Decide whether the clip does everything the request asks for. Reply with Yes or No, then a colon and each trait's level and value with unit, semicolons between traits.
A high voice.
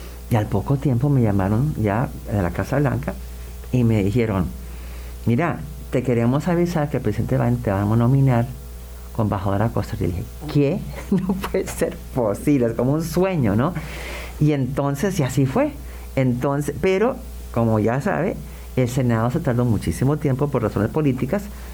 No: low, 120 Hz